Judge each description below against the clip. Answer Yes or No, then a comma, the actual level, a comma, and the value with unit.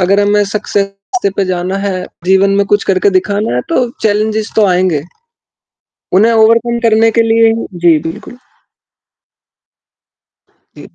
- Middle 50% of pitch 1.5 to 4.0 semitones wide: Yes, average, 2.8 semitones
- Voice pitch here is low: No, high, 205 Hz